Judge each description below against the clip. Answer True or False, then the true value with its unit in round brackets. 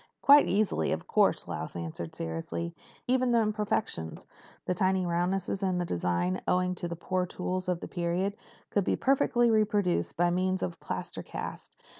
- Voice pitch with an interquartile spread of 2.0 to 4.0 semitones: True (3.3 semitones)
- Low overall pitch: False (180 Hz)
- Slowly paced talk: False (160 wpm)